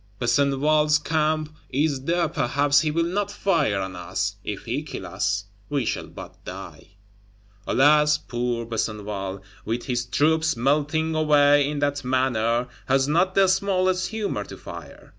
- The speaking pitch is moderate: Yes, medium, 145 Hz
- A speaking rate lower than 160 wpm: Yes, average, 145 wpm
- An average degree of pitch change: Yes, average, 4.7 semitones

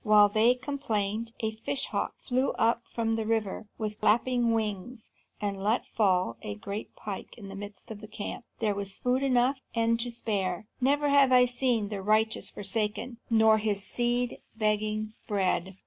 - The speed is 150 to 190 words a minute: Yes, average, 170 wpm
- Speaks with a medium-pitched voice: No, high, 220 Hz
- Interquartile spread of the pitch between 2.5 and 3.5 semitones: Yes, average, 2.8 semitones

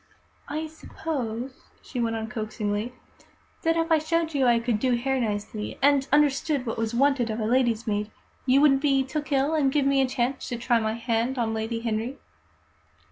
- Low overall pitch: No, very high, 250 Hz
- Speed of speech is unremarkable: Yes, average, 190 wpm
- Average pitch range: Yes, average, 3.7 semitones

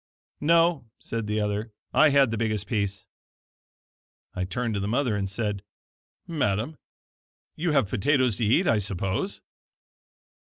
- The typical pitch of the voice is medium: No, low, 110 Hz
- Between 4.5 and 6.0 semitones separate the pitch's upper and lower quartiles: Yes, wide, 5.4 semitones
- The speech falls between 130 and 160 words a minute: Yes, average, 140 wpm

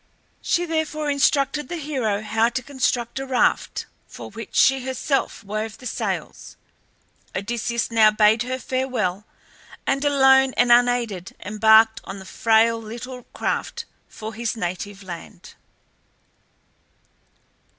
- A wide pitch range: No, average, 3.6 semitones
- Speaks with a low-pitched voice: No, high, 235 Hz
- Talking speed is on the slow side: Yes, slow, 120 wpm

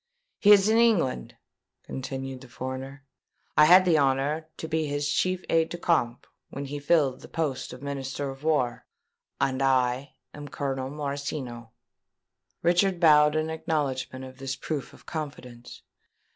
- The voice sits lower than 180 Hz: Yes, medium, 140 Hz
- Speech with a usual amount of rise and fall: Yes, average, 3.2 semitones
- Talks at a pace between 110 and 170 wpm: Yes, average, 150 wpm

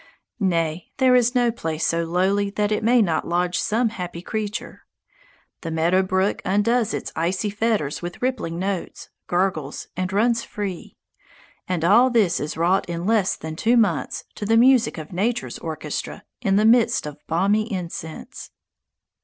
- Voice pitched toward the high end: Yes, high, 195 Hz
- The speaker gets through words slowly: No, average, 160 wpm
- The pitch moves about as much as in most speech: Yes, average, 4.7 semitones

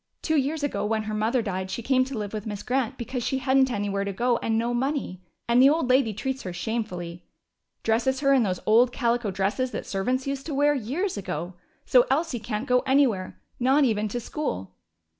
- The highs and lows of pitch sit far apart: No, average, 4.1 semitones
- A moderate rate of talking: No, fast, 210 wpm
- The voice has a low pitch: No, high, 240 Hz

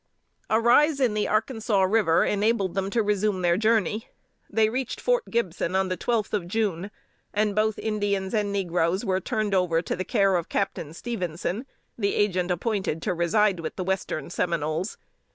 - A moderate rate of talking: Yes, average, 170 wpm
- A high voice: Yes, high, 200 Hz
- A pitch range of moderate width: Yes, average, 3.3 semitones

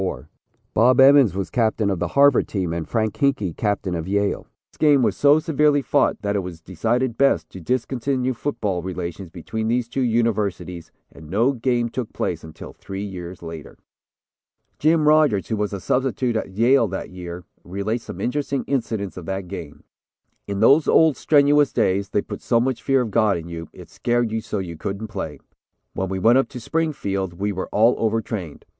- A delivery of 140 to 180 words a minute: No, average, 190 wpm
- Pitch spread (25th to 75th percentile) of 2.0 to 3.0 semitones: No, wide, 5.5 semitones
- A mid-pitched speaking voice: No, low, 110 Hz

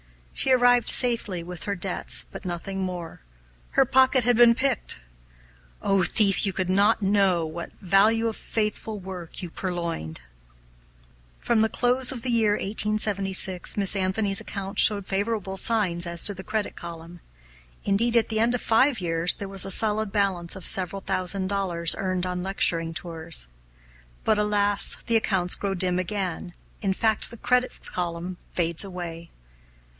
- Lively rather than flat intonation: No, average, 3.5 semitones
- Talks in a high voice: Yes, high, 195 Hz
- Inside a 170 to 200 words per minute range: No, average, 160 wpm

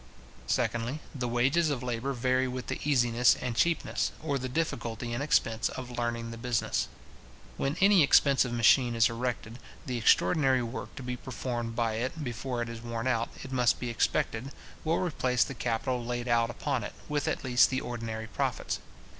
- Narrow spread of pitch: Yes, narrow, 2.2 semitones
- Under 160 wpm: No, average, 180 wpm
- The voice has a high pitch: No, low, 125 Hz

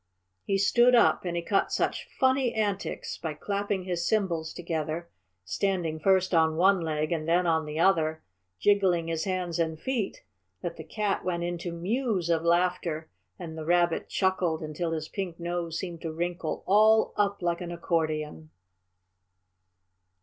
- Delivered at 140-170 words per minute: Yes, average, 155 wpm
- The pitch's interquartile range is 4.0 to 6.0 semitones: No, average, 3.0 semitones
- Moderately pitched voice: Yes, medium, 175 Hz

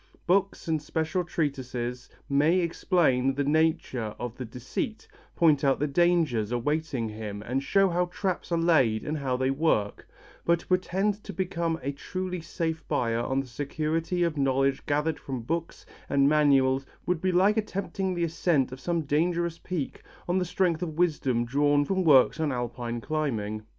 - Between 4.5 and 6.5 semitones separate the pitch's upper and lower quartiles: Yes, average, 4.8 semitones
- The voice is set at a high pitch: No, medium, 150 Hz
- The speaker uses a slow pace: No, average, 170 wpm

